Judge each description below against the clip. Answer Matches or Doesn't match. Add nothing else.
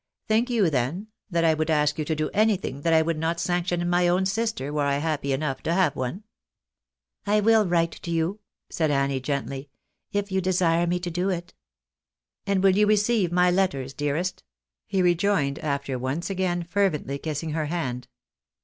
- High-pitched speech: Doesn't match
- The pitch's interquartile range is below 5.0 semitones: Matches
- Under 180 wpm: Doesn't match